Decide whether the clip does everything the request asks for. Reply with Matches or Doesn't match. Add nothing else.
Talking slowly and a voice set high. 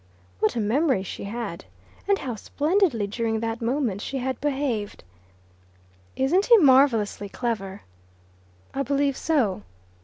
Matches